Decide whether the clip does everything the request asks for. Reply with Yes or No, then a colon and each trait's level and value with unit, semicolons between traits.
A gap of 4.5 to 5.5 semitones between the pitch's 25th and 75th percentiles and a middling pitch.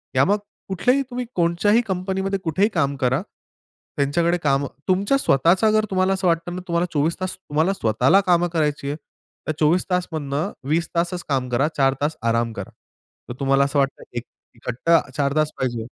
Yes: average, 5.0 semitones; medium, 165 Hz